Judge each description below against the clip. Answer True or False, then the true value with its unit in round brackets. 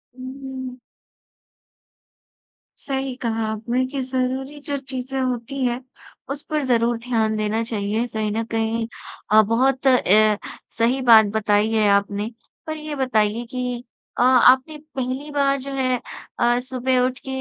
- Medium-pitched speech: False (250 Hz)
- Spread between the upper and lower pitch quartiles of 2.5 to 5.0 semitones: True (2.9 semitones)